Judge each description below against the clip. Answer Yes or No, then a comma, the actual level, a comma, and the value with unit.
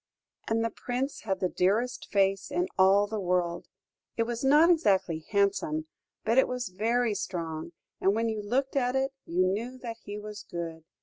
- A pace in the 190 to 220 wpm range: No, average, 180 wpm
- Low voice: No, high, 205 Hz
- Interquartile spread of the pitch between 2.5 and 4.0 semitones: No, average, 4.7 semitones